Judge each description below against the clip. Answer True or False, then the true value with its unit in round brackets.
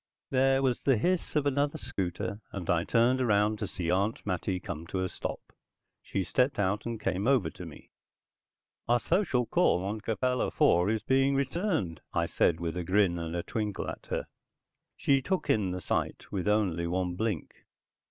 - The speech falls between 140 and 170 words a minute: False (180 wpm)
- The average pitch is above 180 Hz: False (105 Hz)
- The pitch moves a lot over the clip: True (6.0 semitones)